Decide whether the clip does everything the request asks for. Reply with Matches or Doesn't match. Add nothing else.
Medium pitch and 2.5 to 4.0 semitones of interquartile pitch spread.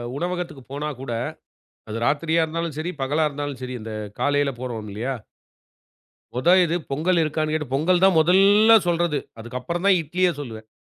Doesn't match